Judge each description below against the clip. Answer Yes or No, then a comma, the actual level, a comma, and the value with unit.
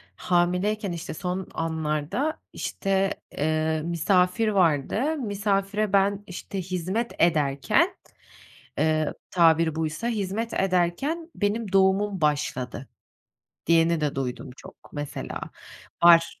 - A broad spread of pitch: No, average, 4.3 semitones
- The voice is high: No, medium, 180 Hz